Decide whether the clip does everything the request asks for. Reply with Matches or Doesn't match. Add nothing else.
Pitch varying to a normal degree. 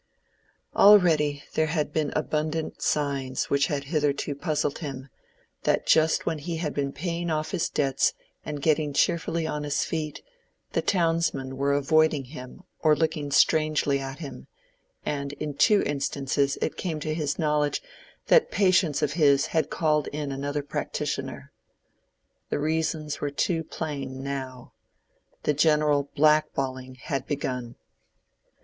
Doesn't match